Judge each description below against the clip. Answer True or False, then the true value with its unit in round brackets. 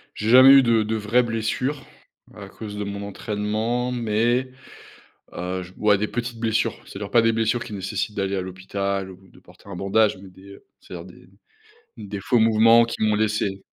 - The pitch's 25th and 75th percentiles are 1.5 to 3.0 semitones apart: True (2.7 semitones)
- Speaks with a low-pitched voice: True (105 Hz)